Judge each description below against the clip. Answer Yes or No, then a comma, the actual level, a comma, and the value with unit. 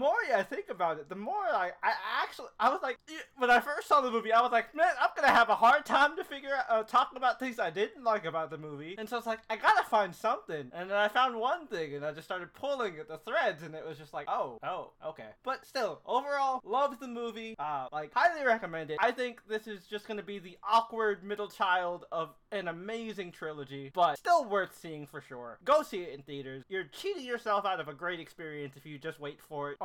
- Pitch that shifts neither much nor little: No, wide, 7.5 semitones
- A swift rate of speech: Yes, fast, 255 wpm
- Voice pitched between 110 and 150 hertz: No, high, 210 Hz